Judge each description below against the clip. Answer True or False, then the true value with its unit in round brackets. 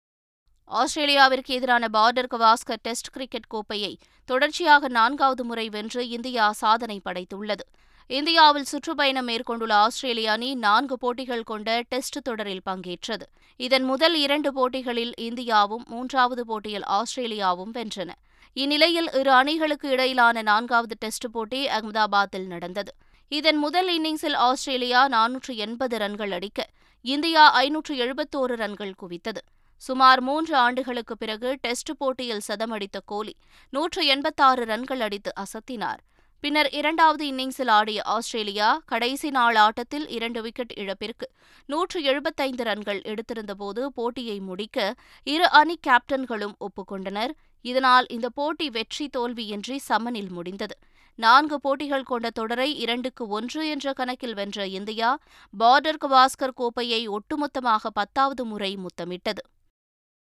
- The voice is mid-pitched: False (245 Hz)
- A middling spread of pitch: True (3.9 semitones)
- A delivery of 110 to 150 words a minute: True (115 wpm)